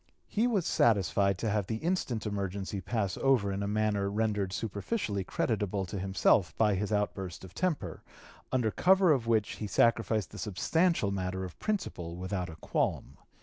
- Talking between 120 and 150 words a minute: No, average, 165 wpm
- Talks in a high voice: No, low, 105 Hz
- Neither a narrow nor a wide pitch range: Yes, average, 3.3 semitones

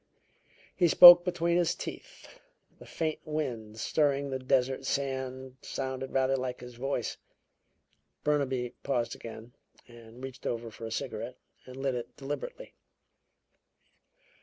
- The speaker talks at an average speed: No, slow, 125 wpm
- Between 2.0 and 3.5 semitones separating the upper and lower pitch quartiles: Yes, average, 3.0 semitones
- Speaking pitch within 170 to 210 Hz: No, low, 130 Hz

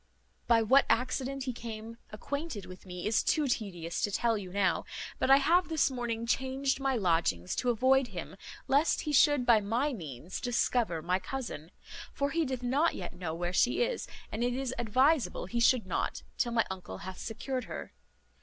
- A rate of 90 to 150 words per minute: No, average, 185 wpm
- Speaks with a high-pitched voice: Yes, high, 235 Hz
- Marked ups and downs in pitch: Yes, wide, 5.9 semitones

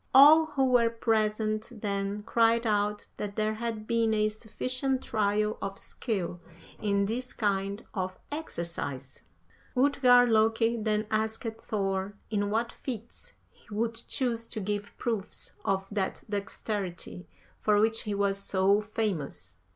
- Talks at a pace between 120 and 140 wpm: Yes, slow, 135 wpm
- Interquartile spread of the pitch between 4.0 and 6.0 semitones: No, narrow, 2.4 semitones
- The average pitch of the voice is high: Yes, high, 215 Hz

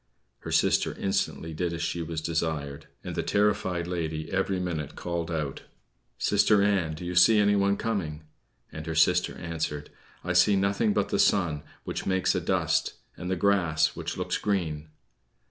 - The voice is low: Yes, very low, 85 Hz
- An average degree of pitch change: Yes, average, 3.7 semitones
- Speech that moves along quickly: No, average, 165 wpm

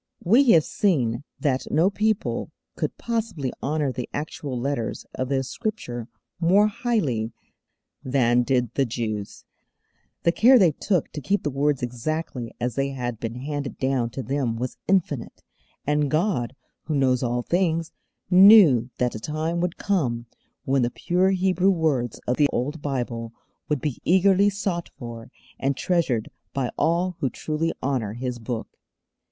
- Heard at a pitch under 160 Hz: Yes, medium, 140 Hz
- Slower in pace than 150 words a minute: No, average, 155 wpm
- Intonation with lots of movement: Yes, wide, 6.1 semitones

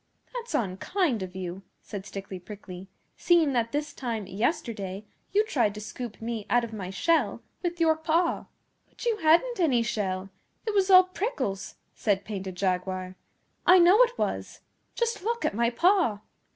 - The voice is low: No, high, 235 Hz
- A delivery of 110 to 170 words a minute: Yes, average, 165 wpm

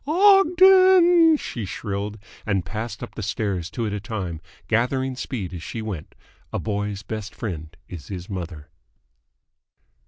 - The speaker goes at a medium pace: Yes, average, 145 wpm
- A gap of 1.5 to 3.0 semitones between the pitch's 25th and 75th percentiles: No, wide, 5.6 semitones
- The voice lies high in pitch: No, low, 105 Hz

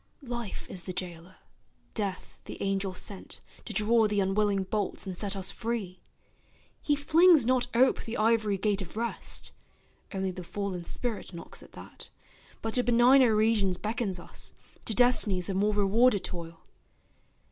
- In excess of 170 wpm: No, average, 155 wpm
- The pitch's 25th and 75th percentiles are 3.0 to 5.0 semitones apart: Yes, average, 3.5 semitones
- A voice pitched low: No, high, 205 Hz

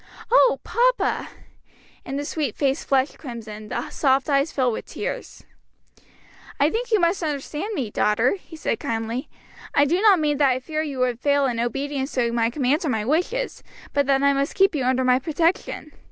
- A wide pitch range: No, average, 3.8 semitones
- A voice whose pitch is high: Yes, very high, 280 Hz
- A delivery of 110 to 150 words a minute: No, average, 185 wpm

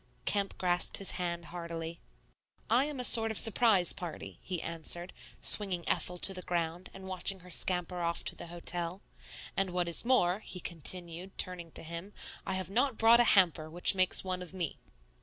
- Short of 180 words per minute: No, average, 185 wpm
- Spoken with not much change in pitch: Yes, narrow, 2.2 semitones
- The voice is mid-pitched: Yes, medium, 180 Hz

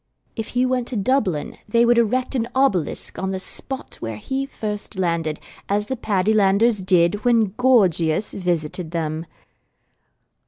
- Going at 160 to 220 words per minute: No, average, 145 wpm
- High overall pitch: Yes, high, 205 Hz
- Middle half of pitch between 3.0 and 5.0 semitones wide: No, wide, 5.6 semitones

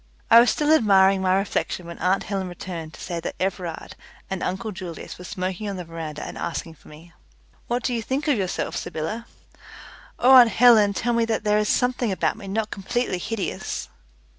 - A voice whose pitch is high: Yes, high, 195 Hz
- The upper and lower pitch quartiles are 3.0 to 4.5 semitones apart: Yes, average, 4.2 semitones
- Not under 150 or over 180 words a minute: No, average, 195 wpm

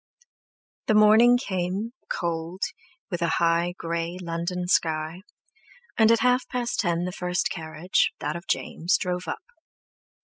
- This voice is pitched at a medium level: Yes, medium, 180 Hz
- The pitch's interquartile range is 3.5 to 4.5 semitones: Yes, average, 3.8 semitones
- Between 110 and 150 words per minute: Yes, average, 140 wpm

